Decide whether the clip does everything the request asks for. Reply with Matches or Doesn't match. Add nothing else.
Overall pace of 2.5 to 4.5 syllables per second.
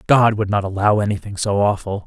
Doesn't match